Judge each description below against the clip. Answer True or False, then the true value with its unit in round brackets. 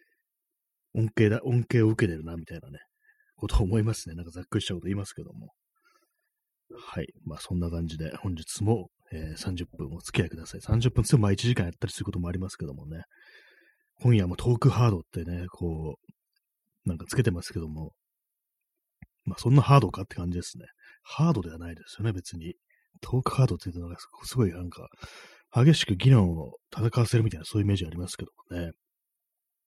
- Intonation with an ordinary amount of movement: False (6.5 semitones)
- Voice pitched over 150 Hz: False (105 Hz)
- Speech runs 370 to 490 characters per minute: True (395 characters per minute)